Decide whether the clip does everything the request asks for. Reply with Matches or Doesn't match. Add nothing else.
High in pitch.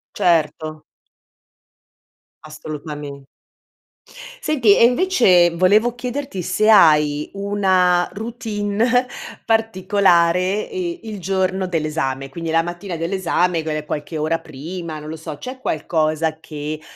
Doesn't match